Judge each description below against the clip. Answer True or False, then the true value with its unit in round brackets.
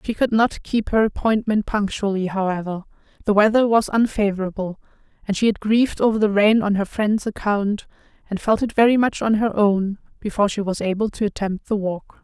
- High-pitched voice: True (210 Hz)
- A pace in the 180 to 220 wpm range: True (190 wpm)